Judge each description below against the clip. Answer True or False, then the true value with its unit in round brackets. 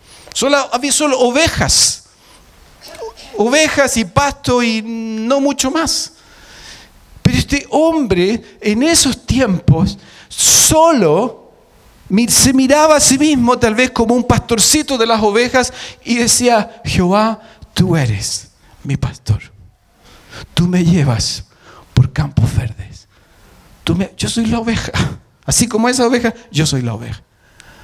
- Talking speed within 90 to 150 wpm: True (125 wpm)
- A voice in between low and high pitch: False (225 Hz)